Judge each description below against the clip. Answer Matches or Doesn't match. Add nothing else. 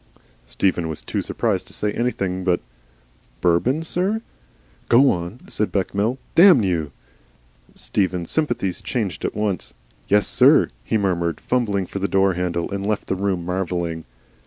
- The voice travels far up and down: Doesn't match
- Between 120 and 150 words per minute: Matches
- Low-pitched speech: Matches